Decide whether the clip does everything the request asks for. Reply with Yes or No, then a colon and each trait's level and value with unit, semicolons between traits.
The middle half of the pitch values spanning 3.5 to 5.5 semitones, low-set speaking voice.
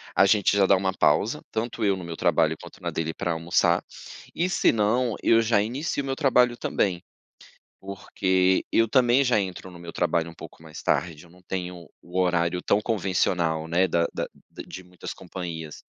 Yes: average, 4.1 semitones; very low, 95 Hz